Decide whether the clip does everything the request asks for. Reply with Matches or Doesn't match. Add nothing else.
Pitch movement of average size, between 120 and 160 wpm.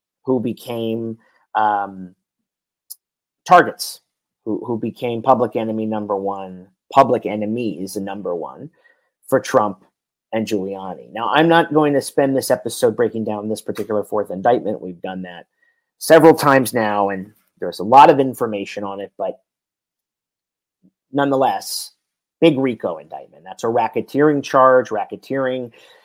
Matches